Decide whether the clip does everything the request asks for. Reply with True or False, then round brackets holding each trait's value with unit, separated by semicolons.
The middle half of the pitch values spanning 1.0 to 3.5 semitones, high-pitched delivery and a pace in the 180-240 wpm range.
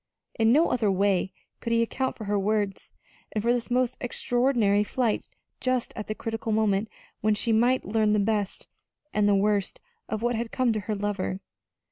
True (2.6 semitones; 220 Hz; 185 wpm)